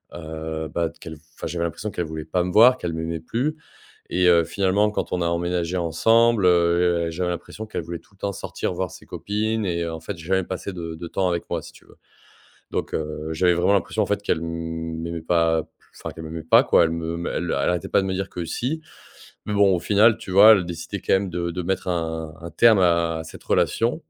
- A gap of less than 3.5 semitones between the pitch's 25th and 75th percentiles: Yes, average, 3.0 semitones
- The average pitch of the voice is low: Yes, very low, 85 Hz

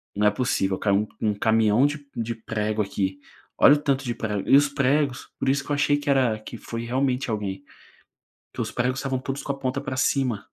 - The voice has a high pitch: No, low, 125 Hz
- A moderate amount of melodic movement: Yes, average, 4.4 semitones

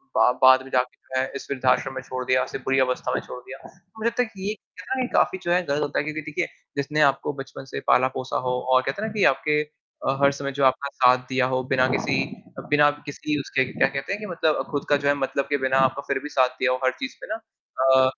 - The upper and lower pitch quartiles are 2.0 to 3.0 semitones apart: Yes, average, 2.7 semitones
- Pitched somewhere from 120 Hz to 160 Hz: Yes, low, 135 Hz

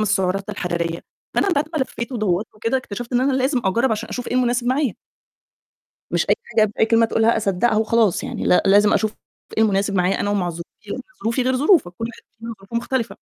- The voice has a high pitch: Yes, high, 220 Hz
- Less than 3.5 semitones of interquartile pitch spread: No, average, 3.8 semitones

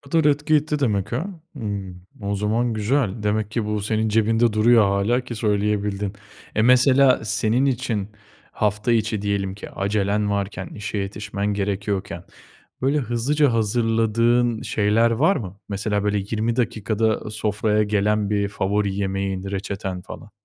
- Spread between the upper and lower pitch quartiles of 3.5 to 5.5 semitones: No, narrow, 2.5 semitones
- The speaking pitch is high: No, low, 105 Hz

